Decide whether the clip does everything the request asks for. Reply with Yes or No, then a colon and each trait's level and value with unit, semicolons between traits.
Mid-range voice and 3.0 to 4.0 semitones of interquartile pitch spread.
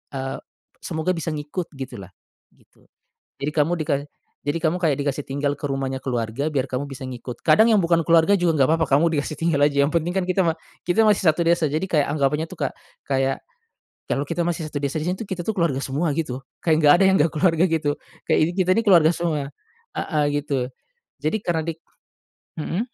Yes: medium, 155 Hz; average, 3.3 semitones